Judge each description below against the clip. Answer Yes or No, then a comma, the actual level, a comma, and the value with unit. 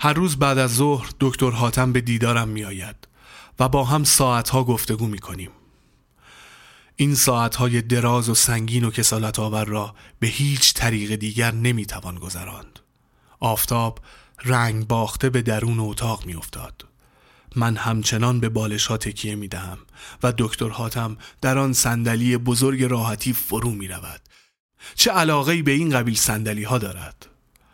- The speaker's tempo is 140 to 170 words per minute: Yes, fast, 155 wpm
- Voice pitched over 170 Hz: No, low, 115 Hz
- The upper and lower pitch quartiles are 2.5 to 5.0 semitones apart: Yes, average, 2.8 semitones